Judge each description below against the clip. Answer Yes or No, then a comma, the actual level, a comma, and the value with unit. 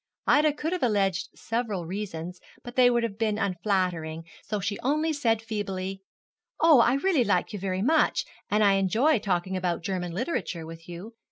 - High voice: Yes, high, 205 Hz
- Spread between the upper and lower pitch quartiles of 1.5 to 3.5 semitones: No, average, 4.8 semitones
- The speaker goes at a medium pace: Yes, average, 175 wpm